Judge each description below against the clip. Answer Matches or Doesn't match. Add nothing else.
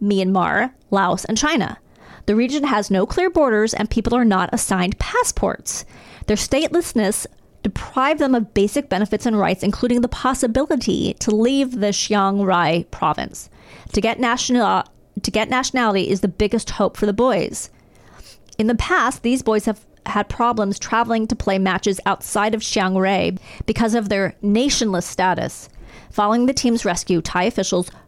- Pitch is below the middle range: Doesn't match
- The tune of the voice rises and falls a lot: Doesn't match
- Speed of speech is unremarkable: Matches